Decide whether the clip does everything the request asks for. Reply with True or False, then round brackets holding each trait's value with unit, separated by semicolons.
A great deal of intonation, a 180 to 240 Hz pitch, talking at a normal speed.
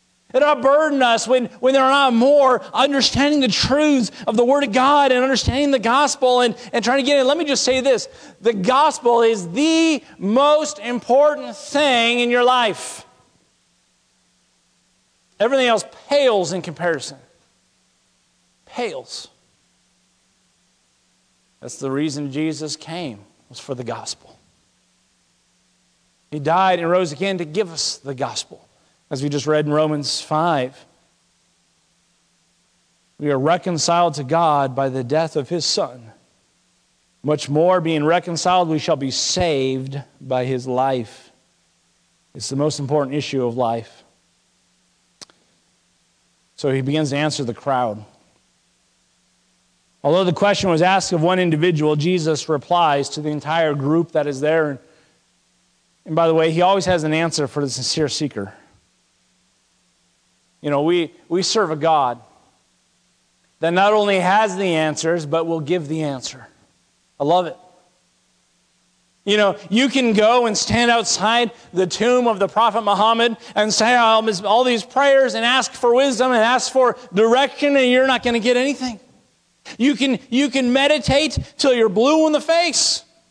True (8.6 semitones; 185 Hz; 150 wpm)